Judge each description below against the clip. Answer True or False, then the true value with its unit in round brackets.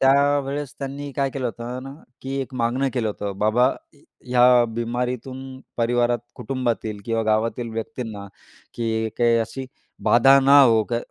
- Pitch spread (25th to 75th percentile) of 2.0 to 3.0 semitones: True (2.7 semitones)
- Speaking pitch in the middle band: False (120 Hz)